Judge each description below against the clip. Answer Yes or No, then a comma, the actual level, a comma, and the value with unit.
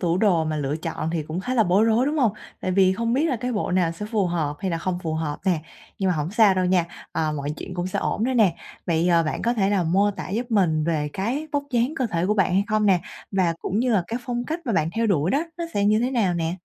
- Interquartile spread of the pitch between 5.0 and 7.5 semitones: Yes, average, 5.3 semitones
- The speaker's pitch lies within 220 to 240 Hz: No, high, 190 Hz